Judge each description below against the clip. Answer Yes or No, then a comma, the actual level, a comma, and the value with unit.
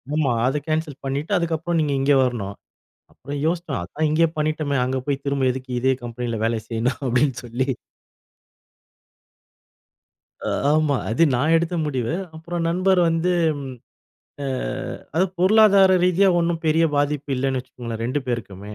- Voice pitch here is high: No, medium, 145 Hz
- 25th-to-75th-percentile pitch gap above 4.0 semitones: Yes, average, 4.6 semitones